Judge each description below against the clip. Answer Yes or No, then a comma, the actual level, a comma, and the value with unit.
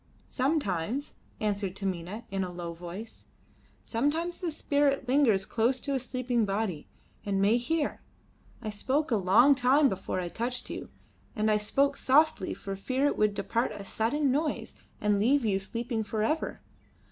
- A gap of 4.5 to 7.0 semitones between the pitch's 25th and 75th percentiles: Yes, wide, 5.6 semitones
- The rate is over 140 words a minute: Yes, average, 165 wpm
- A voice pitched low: No, high, 230 Hz